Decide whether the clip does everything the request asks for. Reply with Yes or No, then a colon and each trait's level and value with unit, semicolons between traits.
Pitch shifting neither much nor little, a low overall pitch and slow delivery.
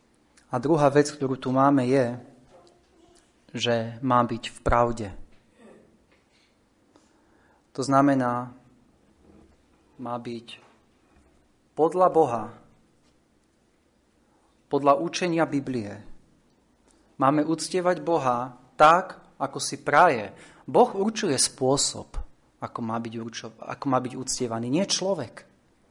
Yes: average, 4.8 semitones; low, 130 Hz; slow, 95 wpm